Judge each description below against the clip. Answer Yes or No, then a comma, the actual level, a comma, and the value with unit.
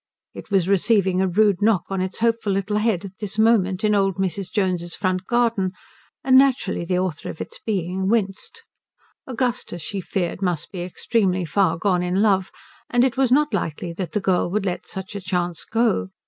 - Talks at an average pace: Yes, average, 190 wpm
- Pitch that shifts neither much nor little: Yes, average, 3.1 semitones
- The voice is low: No, high, 195 Hz